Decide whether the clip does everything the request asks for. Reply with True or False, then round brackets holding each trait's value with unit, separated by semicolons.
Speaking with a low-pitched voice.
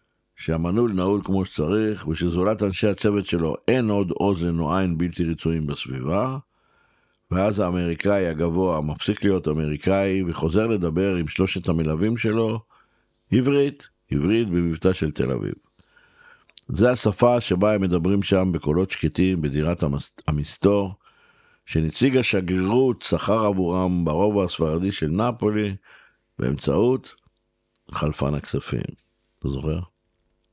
True (95 Hz)